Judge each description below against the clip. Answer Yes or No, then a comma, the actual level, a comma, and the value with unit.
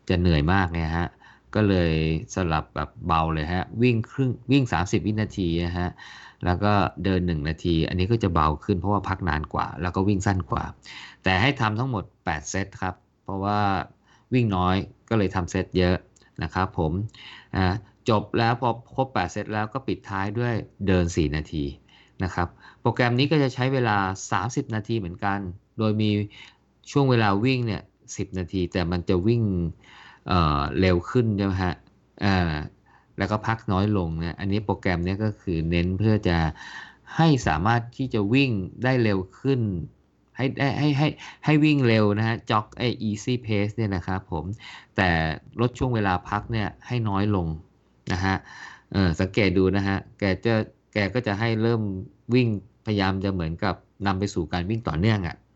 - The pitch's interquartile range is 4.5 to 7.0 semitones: No, average, 3.9 semitones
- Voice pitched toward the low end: Yes, low, 100 Hz